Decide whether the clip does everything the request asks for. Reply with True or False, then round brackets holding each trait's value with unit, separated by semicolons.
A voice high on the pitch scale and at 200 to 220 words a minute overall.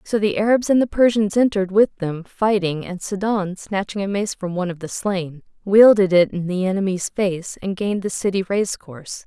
True (195 Hz; 205 wpm)